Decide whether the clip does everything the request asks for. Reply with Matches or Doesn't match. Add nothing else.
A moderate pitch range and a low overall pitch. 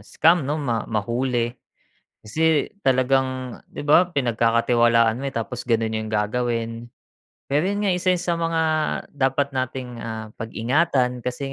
Matches